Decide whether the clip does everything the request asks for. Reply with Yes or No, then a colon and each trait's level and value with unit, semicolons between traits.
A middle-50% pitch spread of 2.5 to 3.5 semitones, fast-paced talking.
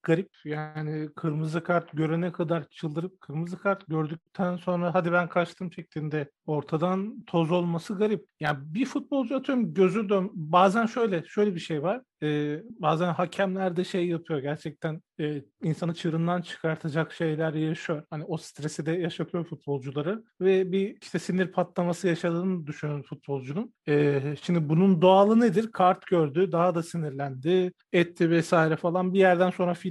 Yes: average, 2.9 semitones; fast, 150 wpm